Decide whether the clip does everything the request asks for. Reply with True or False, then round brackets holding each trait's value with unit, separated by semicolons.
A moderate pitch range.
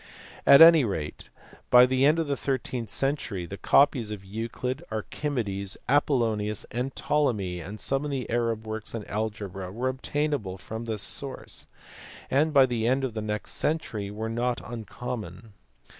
True (4.2 semitones)